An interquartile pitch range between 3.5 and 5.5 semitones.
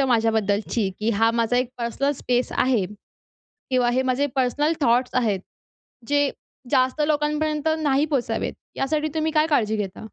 Yes: average, 4.1 semitones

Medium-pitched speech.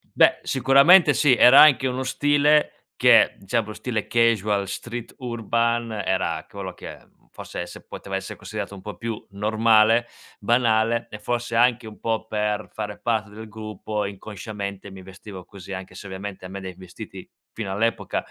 No: low, 110 Hz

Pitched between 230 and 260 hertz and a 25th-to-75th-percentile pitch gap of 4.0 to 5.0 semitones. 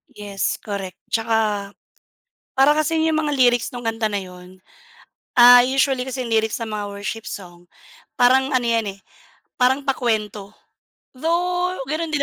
Yes: high, 240 Hz; average, 4.6 semitones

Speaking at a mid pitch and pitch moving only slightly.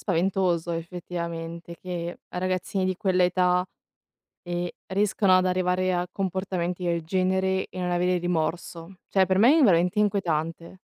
Yes: medium, 180 Hz; narrow, 1.6 semitones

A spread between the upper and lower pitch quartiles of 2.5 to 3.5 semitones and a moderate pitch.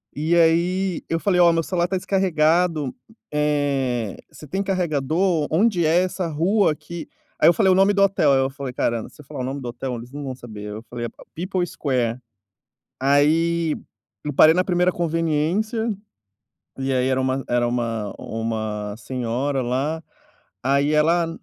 No: average, 5.2 semitones; medium, 150 Hz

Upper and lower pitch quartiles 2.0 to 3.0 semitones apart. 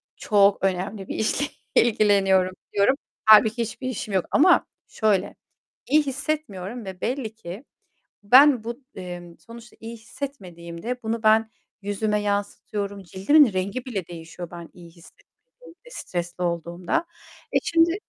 No: average, 4.8 semitones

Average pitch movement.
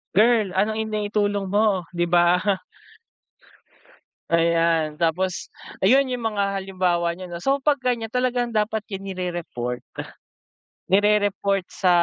Yes: average, 3.8 semitones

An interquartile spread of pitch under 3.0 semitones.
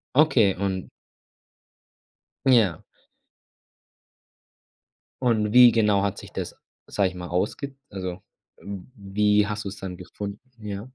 Yes: narrow, 2.6 semitones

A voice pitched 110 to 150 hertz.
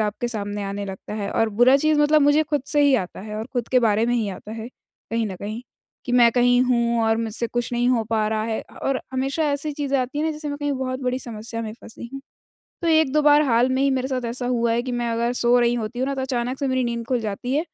No: high, 245 Hz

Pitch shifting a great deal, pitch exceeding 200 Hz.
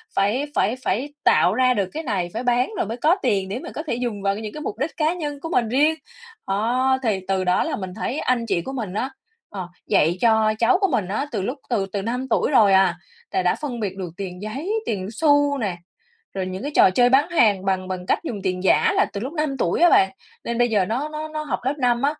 Yes: wide, 6.2 semitones; high, 230 Hz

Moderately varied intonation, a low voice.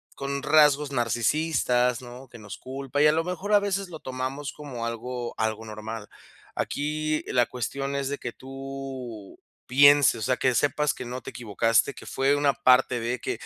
Yes: average, 3.1 semitones; low, 130 Hz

